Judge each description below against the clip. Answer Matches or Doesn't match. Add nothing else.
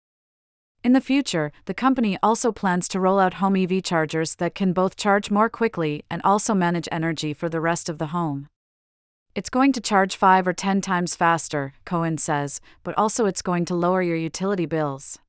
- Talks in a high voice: Doesn't match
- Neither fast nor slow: Matches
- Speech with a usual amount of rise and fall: Matches